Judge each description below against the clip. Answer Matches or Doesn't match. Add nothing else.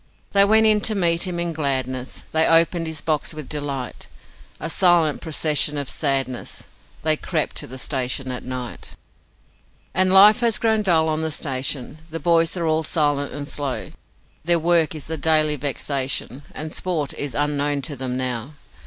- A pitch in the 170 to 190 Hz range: Doesn't match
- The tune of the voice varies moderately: Matches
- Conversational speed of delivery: Matches